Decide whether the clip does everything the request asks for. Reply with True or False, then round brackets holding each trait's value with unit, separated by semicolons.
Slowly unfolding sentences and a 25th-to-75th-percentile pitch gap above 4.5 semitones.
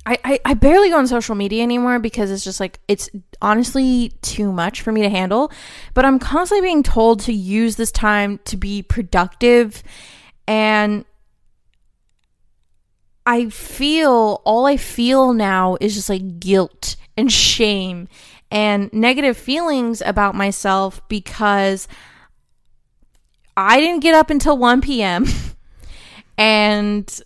False (130 wpm; 3.9 semitones)